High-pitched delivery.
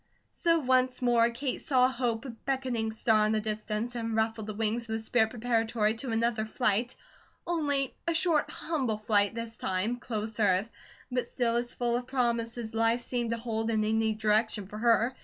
Yes: high, 230 Hz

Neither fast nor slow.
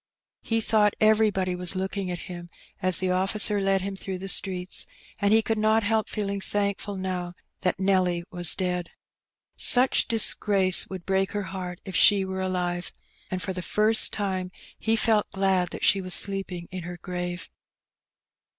Yes: average, 170 wpm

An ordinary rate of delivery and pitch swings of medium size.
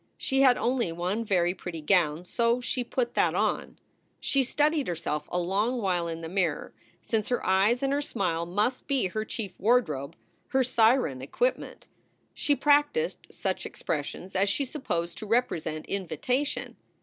No: average, 160 wpm; wide, 6.5 semitones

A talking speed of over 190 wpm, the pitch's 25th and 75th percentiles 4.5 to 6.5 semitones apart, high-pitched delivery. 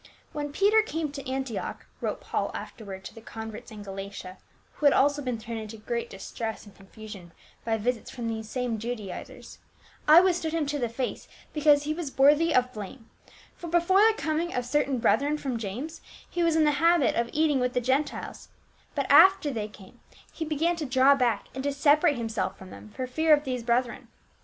Yes: fast, 205 wpm; average, 5.2 semitones; very high, 260 Hz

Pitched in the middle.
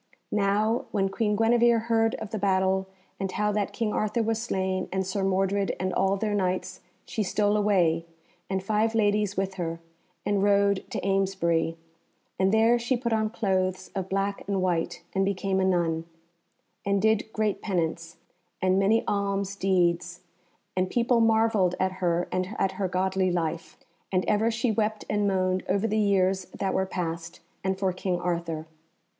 No: high, 195 Hz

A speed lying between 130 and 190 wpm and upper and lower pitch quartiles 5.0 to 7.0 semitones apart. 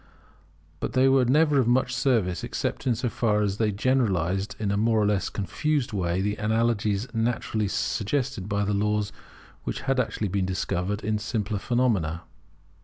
No: average, 165 wpm; average, 3.5 semitones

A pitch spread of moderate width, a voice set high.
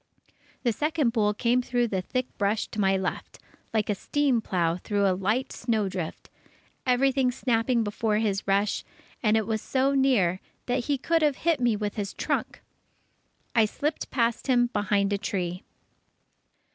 Yes: average, 4.0 semitones; high, 225 Hz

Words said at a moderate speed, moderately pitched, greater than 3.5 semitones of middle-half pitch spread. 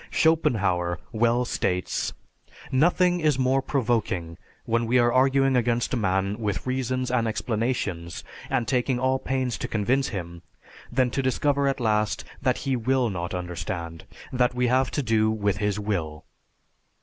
No: average, 150 wpm; low, 120 Hz; average, 4.2 semitones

